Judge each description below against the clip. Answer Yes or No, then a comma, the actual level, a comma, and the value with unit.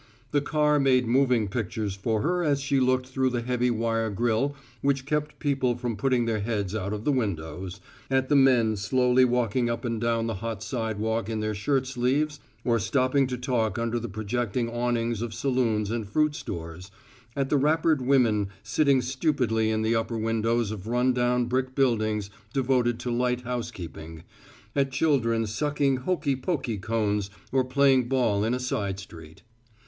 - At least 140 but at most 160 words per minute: No, average, 175 wpm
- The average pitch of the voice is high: No, low, 120 Hz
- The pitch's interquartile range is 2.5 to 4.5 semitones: Yes, average, 3.3 semitones